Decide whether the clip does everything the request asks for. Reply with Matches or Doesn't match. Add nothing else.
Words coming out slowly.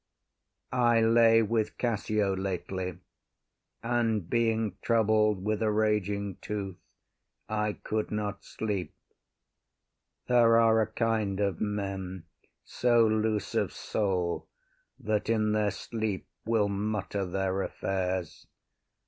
Matches